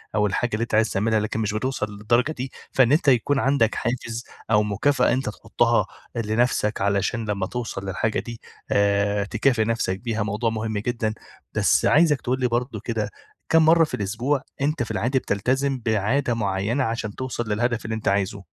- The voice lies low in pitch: Yes, low, 115 Hz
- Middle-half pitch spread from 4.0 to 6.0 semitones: No, average, 3.1 semitones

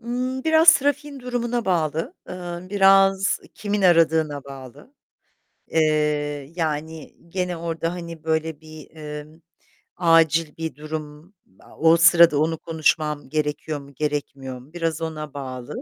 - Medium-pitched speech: Yes, medium, 160 Hz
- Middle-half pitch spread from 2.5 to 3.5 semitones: Yes, average, 3.2 semitones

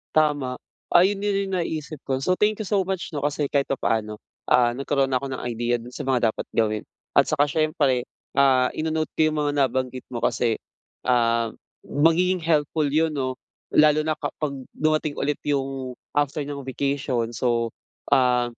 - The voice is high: No, medium, 140 Hz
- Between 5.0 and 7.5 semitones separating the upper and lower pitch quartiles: No, average, 3.5 semitones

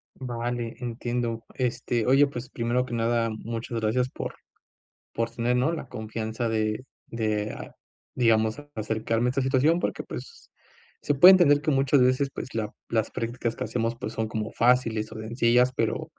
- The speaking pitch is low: Yes, low, 120 Hz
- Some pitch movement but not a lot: No, narrow, 2.2 semitones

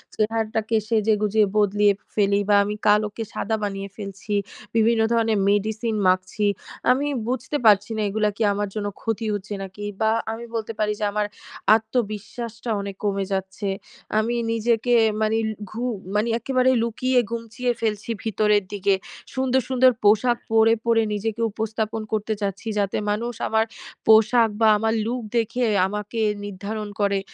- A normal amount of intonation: No, narrow, 1.8 semitones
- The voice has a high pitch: Yes, high, 220 Hz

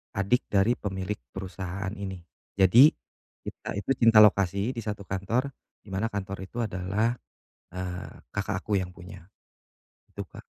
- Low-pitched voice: Yes, low, 100 Hz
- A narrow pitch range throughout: Yes, narrow, 2.3 semitones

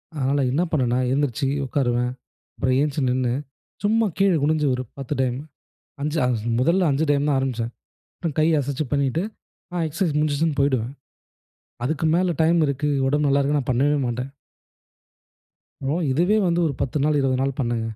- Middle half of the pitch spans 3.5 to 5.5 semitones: No, average, 3.0 semitones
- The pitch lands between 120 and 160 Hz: Yes, medium, 140 Hz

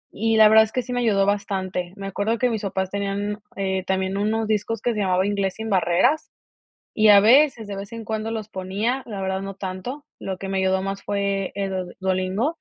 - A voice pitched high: Yes, high, 200 Hz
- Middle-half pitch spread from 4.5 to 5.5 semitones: No, narrow, 2.5 semitones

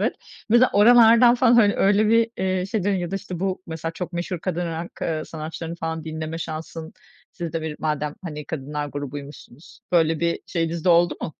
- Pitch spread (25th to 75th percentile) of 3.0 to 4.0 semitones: Yes, average, 3.5 semitones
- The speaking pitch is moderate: Yes, medium, 170 Hz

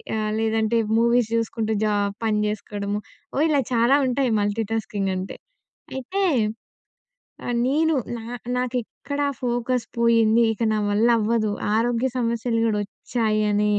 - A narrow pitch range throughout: Yes, narrow, 2.3 semitones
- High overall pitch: Yes, high, 225 Hz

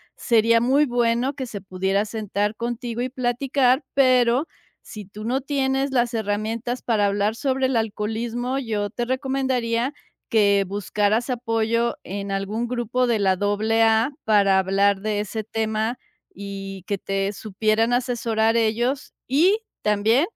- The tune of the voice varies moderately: Yes, average, 3.2 semitones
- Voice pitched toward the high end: Yes, high, 225 Hz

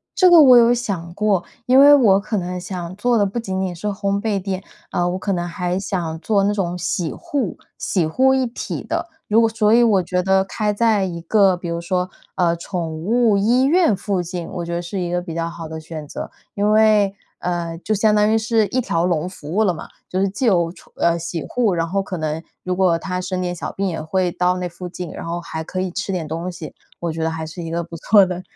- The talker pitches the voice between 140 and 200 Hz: Yes, medium, 185 Hz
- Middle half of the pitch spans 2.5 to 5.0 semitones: Yes, average, 3.5 semitones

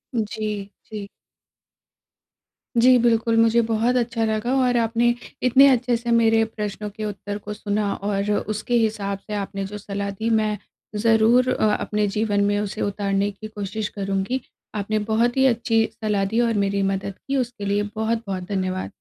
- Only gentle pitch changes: Yes, narrow, 2.2 semitones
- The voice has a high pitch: Yes, high, 215 Hz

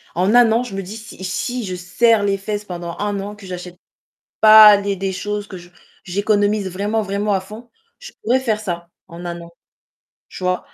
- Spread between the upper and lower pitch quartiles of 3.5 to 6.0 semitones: No, average, 2.8 semitones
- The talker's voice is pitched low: No, high, 200 Hz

